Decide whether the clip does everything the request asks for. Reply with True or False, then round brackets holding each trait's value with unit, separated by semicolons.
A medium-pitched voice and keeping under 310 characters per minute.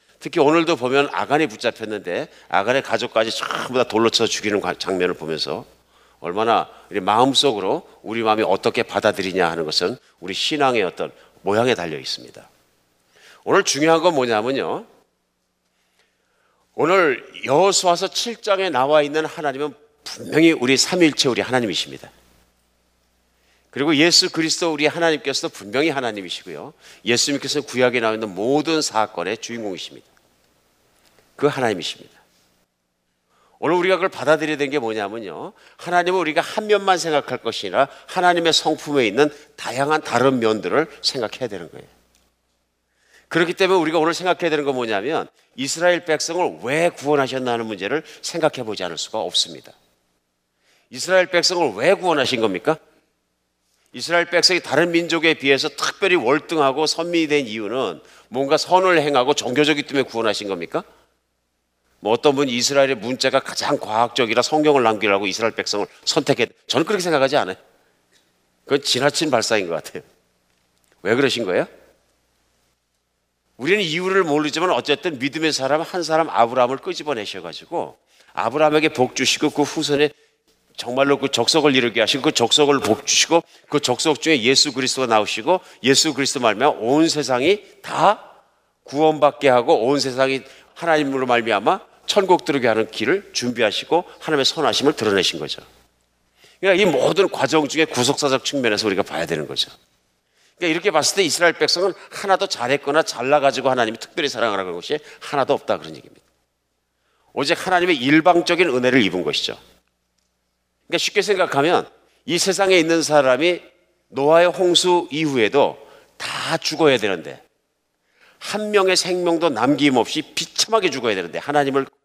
False (145 Hz; 360 characters per minute)